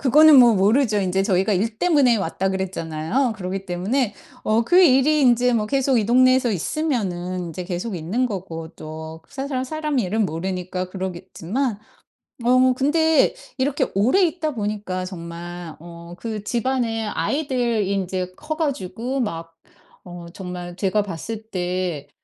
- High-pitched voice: Yes, high, 210 Hz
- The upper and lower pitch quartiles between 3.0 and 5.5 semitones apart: No, wide, 6.1 semitones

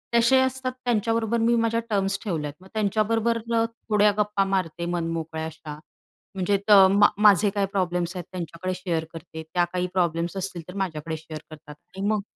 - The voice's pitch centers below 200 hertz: Yes, high, 190 Hz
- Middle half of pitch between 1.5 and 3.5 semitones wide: No, average, 4.1 semitones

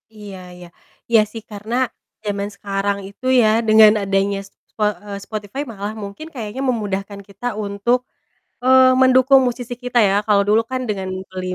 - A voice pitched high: Yes, high, 210 Hz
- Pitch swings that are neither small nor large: Yes, average, 3.3 semitones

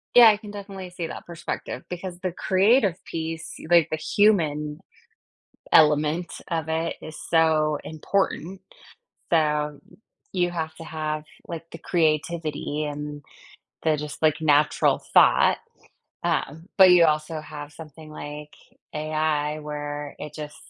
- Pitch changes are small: Yes, narrow, 2.3 semitones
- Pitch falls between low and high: Yes, medium, 155 Hz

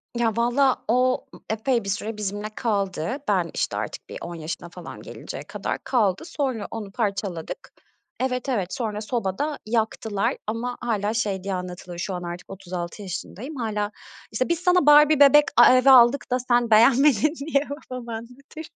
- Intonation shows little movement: No, average, 4.5 semitones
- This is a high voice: Yes, high, 225 Hz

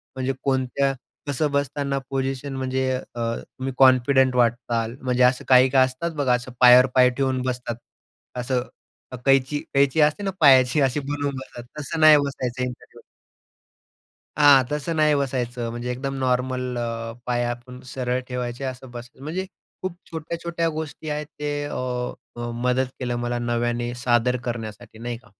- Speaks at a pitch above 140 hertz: No, low, 130 Hz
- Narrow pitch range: Yes, narrow, 2.3 semitones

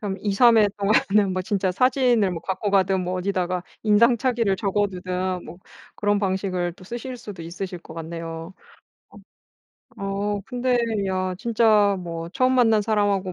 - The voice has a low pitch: No, high, 195 Hz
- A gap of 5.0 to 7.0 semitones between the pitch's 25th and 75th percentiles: No, average, 2.9 semitones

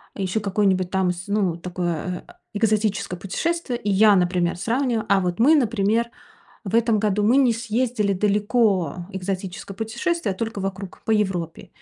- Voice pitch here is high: Yes, high, 205 Hz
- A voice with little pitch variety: No, average, 3.4 semitones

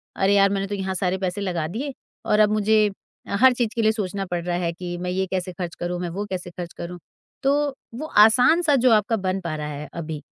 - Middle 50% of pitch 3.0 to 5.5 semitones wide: Yes, average, 3.5 semitones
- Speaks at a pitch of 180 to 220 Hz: Yes, high, 190 Hz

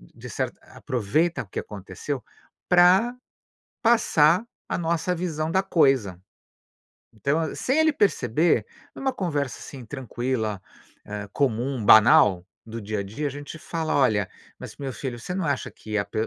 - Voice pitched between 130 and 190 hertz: Yes, medium, 140 Hz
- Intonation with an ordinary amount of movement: No, wide, 7.5 semitones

